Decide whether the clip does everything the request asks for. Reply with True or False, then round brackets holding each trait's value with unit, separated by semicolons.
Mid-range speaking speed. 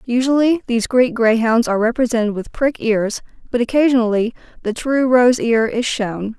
True (160 wpm)